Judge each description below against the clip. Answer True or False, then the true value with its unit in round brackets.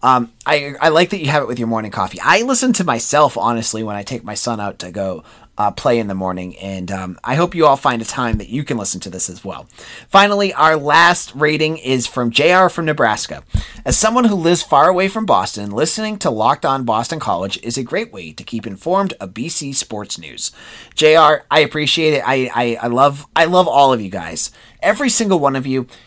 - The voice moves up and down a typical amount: False (6.2 semitones)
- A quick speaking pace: True (230 wpm)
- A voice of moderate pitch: False (130 Hz)